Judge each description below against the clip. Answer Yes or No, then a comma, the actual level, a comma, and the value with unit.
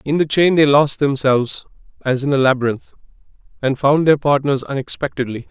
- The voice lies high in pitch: No, medium, 140 Hz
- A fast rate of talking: No, average, 165 wpm